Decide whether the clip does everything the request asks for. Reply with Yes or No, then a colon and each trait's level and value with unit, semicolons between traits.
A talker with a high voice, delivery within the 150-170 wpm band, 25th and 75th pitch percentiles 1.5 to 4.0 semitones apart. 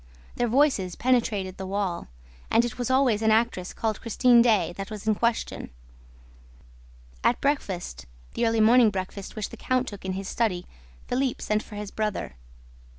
Yes: high, 220 Hz; average, 165 wpm; average, 3.6 semitones